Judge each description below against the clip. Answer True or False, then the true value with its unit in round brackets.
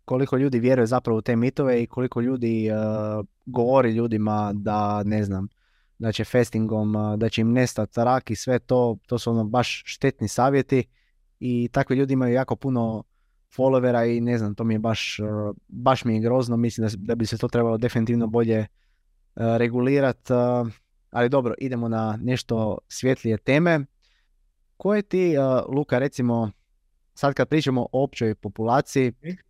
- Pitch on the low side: True (120 Hz)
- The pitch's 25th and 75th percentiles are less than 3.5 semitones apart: True (2.9 semitones)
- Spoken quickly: True (170 wpm)